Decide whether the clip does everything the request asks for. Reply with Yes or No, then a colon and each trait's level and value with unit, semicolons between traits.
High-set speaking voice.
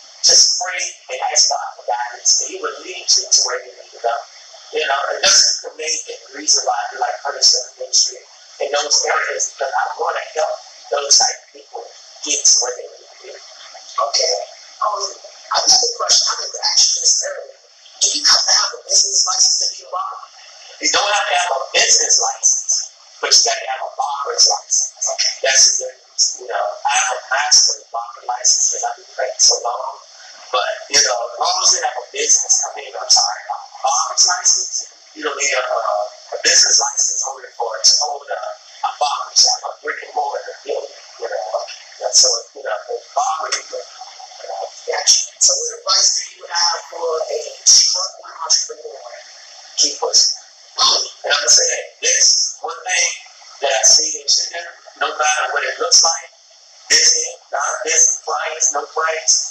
Yes: very high, 390 Hz